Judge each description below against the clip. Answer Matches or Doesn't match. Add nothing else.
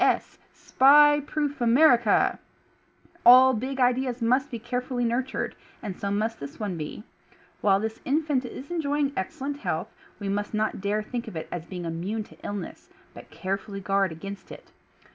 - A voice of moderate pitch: Doesn't match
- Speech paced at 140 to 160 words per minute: Doesn't match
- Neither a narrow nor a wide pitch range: Matches